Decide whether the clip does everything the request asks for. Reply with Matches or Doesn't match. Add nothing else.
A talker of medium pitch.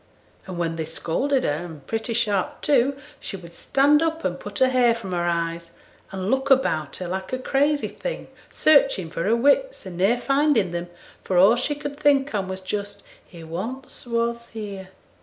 Doesn't match